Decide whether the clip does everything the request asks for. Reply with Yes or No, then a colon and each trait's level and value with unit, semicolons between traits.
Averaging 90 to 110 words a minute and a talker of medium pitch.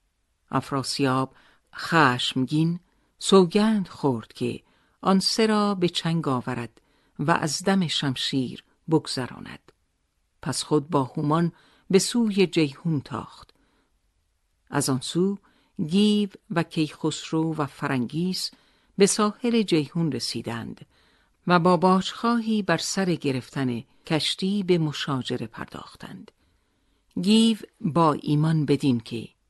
Yes: slow, 105 wpm; medium, 160 Hz